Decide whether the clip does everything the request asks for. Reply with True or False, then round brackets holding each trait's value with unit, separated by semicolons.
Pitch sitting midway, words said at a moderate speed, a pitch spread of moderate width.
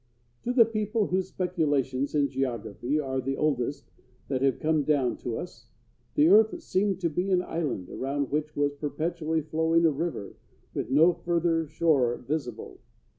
True (150 Hz; 160 wpm; 3.9 semitones)